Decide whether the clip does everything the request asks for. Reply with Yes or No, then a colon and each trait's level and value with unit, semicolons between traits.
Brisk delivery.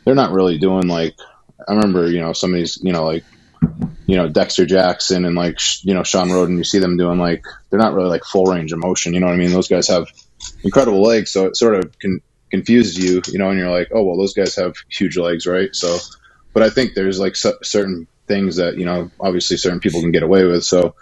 Yes: fast, 245 wpm